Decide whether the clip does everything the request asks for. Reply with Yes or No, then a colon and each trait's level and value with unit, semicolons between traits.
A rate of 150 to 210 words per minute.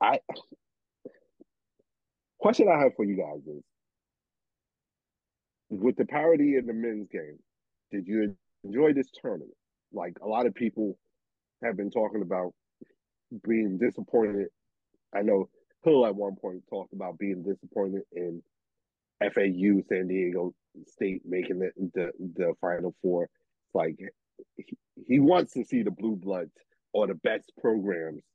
No: average, 140 wpm